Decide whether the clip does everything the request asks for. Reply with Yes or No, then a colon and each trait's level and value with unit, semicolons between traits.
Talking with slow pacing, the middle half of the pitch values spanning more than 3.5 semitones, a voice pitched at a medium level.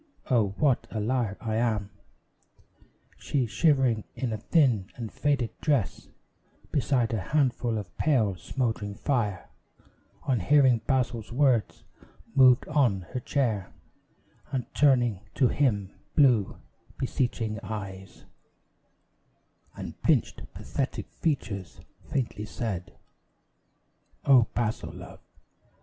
No: slow, 105 wpm; average, 4.0 semitones; low, 120 Hz